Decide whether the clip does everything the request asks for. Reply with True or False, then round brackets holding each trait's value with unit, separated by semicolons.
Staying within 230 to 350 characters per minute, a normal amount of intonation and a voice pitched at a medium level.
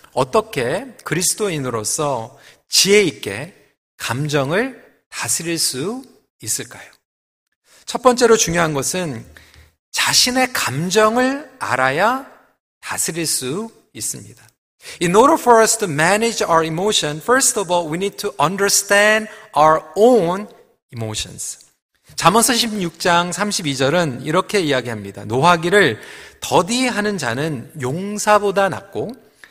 False (315 characters per minute; 6.7 semitones; 180 Hz)